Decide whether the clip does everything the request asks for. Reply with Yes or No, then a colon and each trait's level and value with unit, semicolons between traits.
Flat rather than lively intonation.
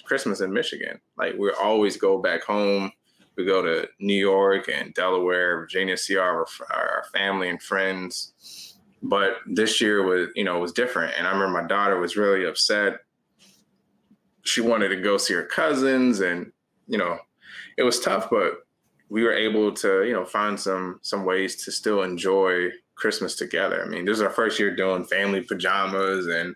Yes: narrow, 2.1 semitones